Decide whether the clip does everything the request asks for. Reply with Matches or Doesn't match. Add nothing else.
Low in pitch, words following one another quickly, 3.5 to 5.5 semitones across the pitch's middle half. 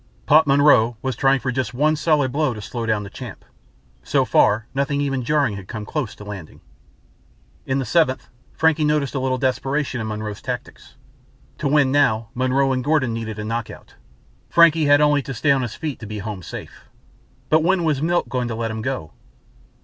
Doesn't match